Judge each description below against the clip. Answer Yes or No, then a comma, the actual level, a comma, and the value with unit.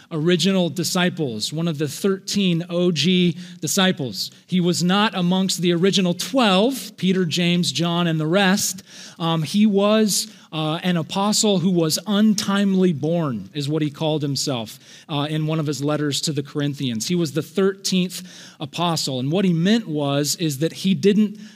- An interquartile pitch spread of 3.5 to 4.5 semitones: Yes, average, 3.8 semitones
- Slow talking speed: No, average, 165 wpm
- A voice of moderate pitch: Yes, medium, 175 Hz